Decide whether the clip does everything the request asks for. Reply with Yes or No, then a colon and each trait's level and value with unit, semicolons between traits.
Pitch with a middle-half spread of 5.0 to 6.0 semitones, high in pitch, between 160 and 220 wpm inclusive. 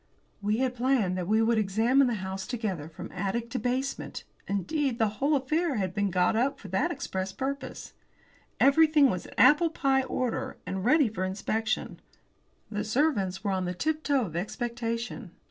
Yes: wide, 5.6 semitones; high, 225 Hz; average, 170 wpm